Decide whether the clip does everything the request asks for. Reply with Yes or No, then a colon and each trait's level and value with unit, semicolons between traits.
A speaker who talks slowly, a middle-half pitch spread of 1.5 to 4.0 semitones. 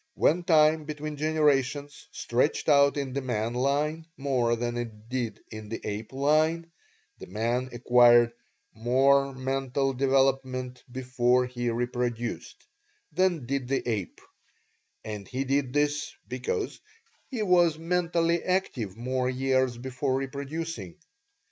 Yes: slow, 125 wpm; average, 3.6 semitones